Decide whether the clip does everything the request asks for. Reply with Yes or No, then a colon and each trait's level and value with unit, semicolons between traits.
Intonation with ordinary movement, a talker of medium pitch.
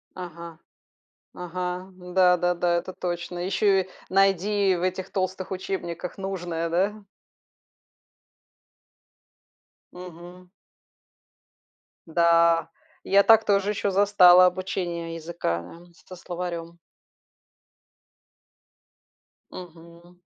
No: narrow, 1.8 semitones; medium, 180 Hz